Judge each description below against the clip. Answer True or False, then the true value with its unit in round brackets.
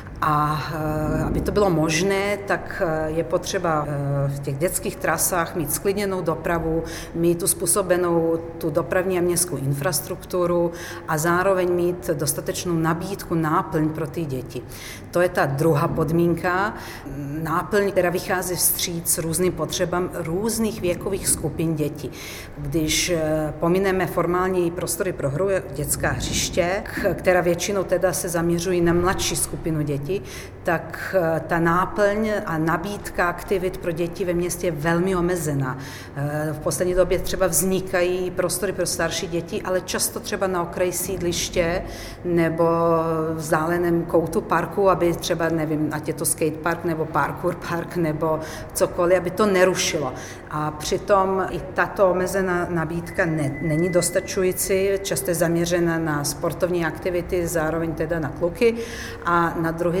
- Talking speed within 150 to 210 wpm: False (135 wpm)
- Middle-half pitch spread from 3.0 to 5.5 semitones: False (2.4 semitones)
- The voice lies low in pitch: False (170 Hz)